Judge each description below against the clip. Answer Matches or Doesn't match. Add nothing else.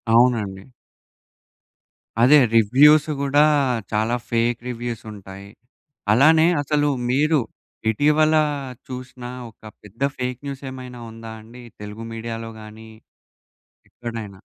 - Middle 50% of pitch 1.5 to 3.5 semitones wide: Doesn't match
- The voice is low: Matches